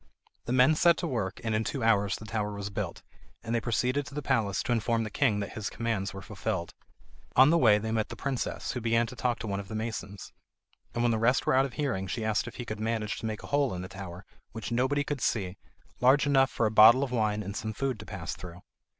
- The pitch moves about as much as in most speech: Yes, average, 3.5 semitones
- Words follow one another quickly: Yes, fast, 260 wpm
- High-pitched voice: No, low, 115 Hz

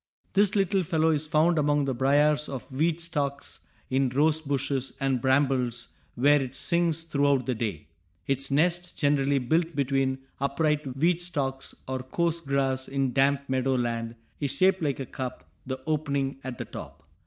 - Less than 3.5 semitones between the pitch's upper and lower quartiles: Yes, average, 2.9 semitones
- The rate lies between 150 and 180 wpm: Yes, average, 165 wpm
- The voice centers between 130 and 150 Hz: Yes, medium, 140 Hz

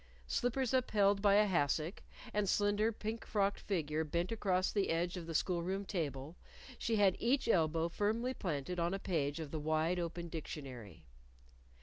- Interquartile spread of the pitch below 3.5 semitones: No, average, 4.4 semitones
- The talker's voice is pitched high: No, medium, 180 Hz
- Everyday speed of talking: Yes, average, 170 wpm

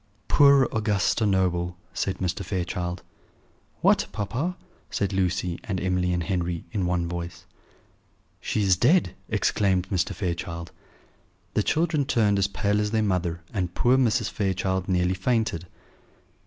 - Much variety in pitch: No, average, 3.1 semitones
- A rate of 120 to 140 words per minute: Yes, slow, 135 wpm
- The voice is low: Yes, very low, 95 Hz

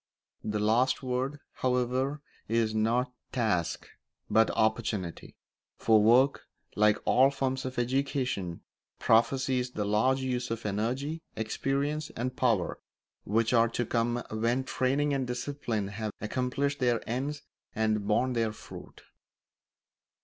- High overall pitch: No, low, 120 Hz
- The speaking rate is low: Yes, slow, 120 wpm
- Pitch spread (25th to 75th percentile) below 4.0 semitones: Yes, average, 3.2 semitones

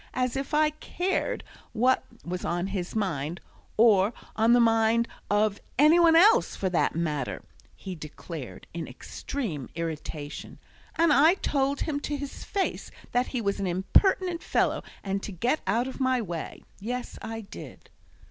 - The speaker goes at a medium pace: Yes, average, 155 wpm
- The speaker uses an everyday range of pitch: No, wide, 7.6 semitones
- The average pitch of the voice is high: Yes, high, 225 Hz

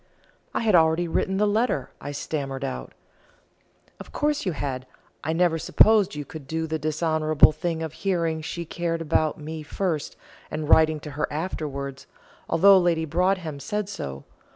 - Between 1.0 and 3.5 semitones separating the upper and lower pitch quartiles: Yes, average, 2.9 semitones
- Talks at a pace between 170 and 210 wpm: No, average, 160 wpm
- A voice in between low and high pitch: Yes, medium, 160 Hz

